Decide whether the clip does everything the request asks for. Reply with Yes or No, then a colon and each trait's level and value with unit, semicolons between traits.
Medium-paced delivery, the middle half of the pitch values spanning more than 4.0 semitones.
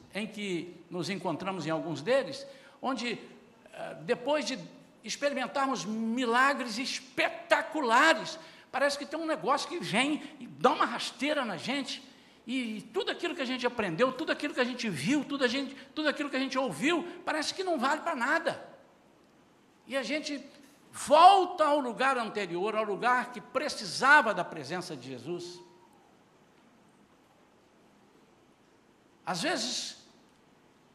Yes: average, 140 wpm; average, 4.5 semitones